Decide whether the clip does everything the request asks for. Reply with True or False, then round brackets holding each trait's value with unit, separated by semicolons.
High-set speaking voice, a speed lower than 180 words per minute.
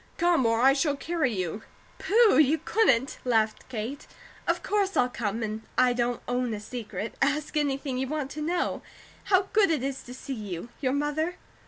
False (270 Hz; 185 wpm)